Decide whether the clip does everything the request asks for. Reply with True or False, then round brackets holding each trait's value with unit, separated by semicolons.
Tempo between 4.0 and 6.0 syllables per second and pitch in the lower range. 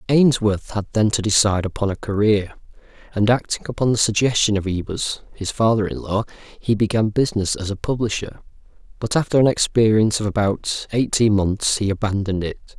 True (5.5 syllables/s; 105 Hz)